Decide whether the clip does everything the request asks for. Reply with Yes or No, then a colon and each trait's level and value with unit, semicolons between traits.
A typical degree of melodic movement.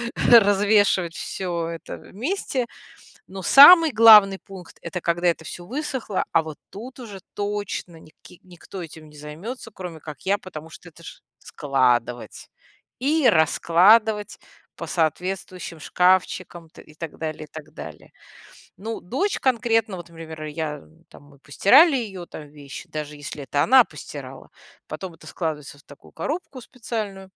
No: wide, 5.7 semitones